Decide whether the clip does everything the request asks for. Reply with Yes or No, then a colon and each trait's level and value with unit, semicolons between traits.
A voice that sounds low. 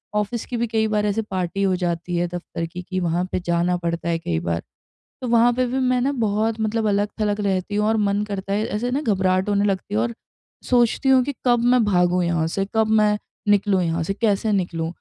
No: high, 205 Hz